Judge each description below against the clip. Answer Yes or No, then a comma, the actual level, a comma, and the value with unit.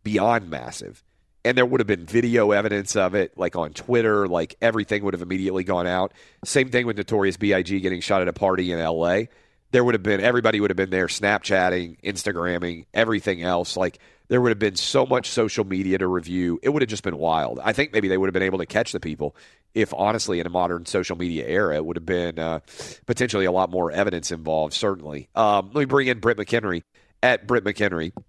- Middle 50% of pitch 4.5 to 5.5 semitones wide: No, average, 3.3 semitones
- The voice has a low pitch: Yes, very low, 95 Hz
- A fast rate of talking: Yes, fast, 225 wpm